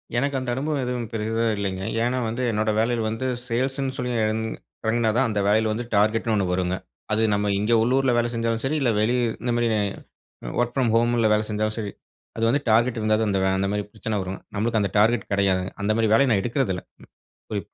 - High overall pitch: No, low, 115 Hz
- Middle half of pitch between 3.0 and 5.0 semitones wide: No, narrow, 2.4 semitones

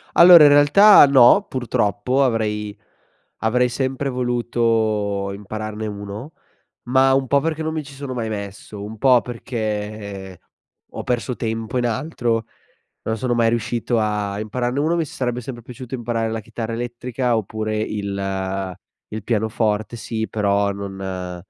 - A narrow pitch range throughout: No, average, 3.3 semitones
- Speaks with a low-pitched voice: Yes, low, 115 Hz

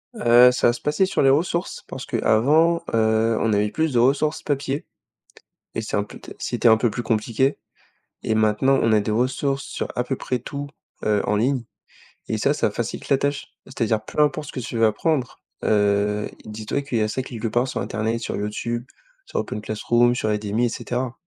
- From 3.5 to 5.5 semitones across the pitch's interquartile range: Yes, average, 3.9 semitones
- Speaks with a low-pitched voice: Yes, low, 120 Hz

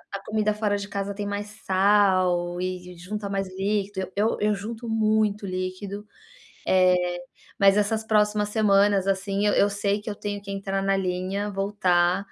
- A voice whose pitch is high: Yes, high, 200 Hz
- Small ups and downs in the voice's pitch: Yes, narrow, 1.5 semitones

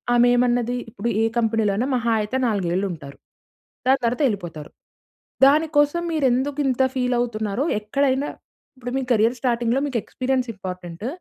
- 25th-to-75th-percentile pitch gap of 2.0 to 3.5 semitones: No, average, 3.9 semitones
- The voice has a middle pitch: No, high, 240 Hz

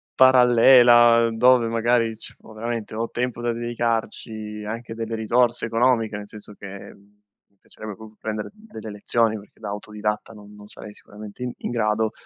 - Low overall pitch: Yes, low, 115 Hz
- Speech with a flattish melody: Yes, narrow, 1.9 semitones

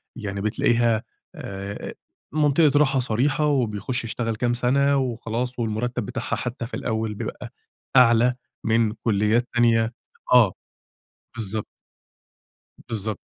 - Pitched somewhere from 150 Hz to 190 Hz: No, low, 115 Hz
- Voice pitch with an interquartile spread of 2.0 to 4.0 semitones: Yes, narrow, 2.4 semitones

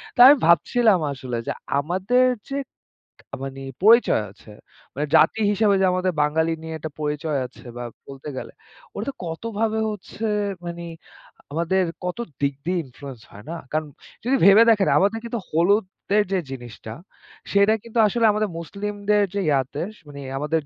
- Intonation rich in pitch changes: Yes, wide, 6.1 semitones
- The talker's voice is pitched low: No, medium, 180 Hz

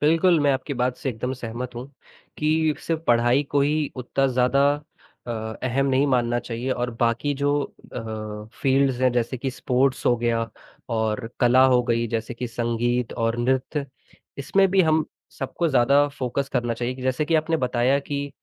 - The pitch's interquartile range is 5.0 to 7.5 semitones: No, average, 2.8 semitones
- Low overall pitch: Yes, low, 130 Hz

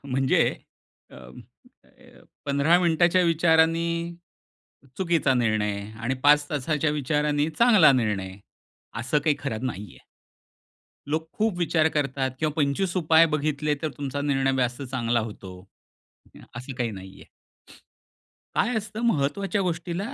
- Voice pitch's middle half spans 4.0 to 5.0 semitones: Yes, average, 4.6 semitones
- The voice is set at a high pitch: No, medium, 145 Hz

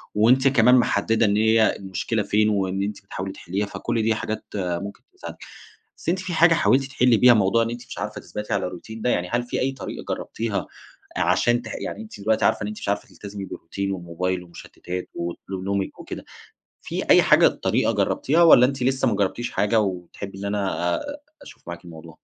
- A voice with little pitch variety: No, average, 3.8 semitones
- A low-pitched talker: Yes, low, 105 Hz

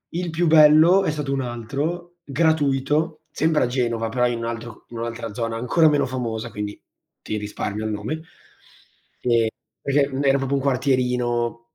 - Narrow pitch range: No, average, 4.6 semitones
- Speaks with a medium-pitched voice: No, low, 130 Hz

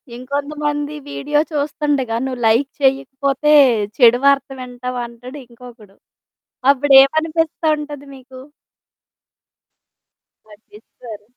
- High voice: Yes, very high, 270 Hz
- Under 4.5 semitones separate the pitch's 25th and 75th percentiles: Yes, average, 2.9 semitones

